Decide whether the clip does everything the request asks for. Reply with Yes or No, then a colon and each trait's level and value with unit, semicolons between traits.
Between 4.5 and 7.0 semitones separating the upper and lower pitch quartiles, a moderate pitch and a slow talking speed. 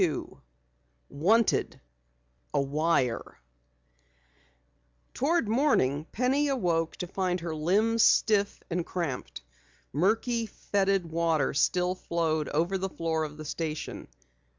Yes: average, 4.8 semitones; medium, 175 Hz; slow, 110 wpm